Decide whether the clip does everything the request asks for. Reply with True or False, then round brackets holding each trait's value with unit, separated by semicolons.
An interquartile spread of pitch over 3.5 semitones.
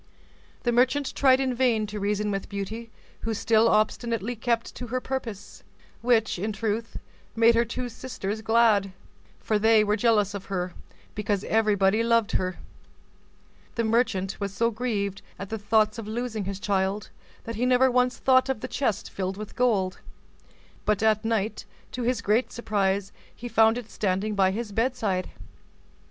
False (2.7 semitones)